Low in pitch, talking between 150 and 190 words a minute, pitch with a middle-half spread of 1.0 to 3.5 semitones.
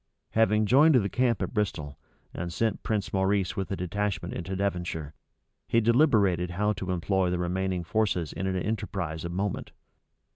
Yes: very low, 95 Hz; average, 160 wpm; average, 3.2 semitones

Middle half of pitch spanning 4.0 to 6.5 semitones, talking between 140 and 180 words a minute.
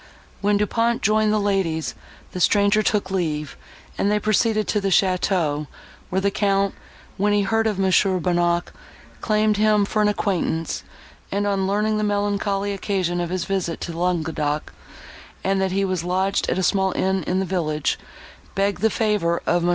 No: narrow, 2.6 semitones; average, 175 wpm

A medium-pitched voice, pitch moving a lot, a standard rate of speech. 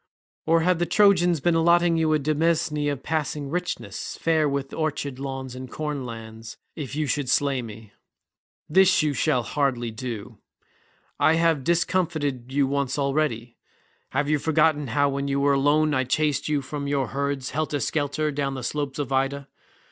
No: medium, 145 Hz; narrow, 2.6 semitones; average, 170 wpm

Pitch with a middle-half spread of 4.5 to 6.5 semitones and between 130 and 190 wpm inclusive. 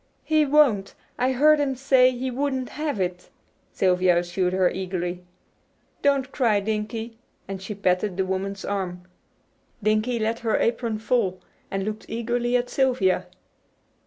Yes: average, 5.0 semitones; average, 140 wpm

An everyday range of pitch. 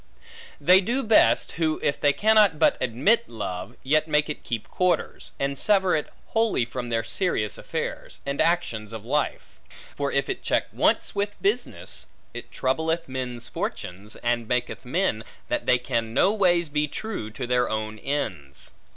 No: wide, 7.4 semitones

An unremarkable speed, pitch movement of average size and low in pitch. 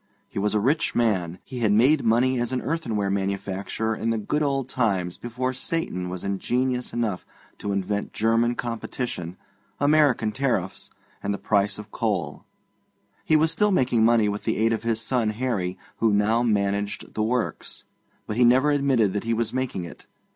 Yes: average, 175 wpm; average, 3.8 semitones; low, 115 Hz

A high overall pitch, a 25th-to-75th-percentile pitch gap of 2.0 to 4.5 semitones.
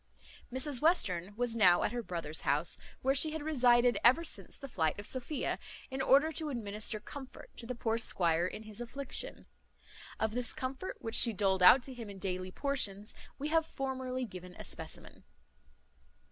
No: high, 240 Hz; average, 5.2 semitones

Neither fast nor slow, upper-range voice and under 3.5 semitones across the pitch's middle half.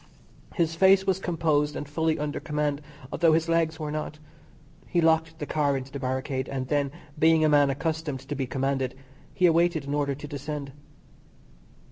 No: average, 175 wpm; medium, 150 Hz; narrow, 2.5 semitones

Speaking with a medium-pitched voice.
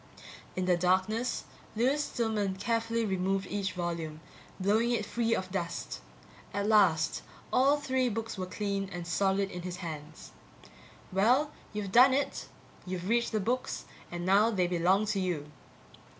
No: high, 195 Hz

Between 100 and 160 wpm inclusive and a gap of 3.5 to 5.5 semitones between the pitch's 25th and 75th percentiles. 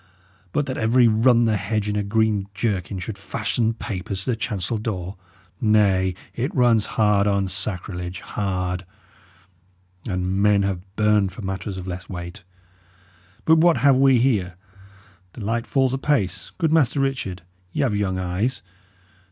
Yes: average, 150 wpm; average, 3.9 semitones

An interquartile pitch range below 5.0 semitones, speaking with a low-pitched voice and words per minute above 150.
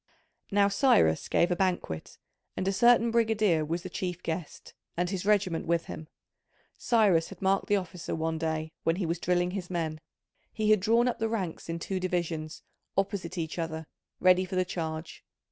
No: average, 3.3 semitones; medium, 180 Hz; average, 180 wpm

